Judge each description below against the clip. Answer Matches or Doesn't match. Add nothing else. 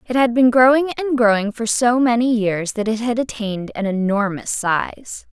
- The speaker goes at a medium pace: Matches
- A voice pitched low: Doesn't match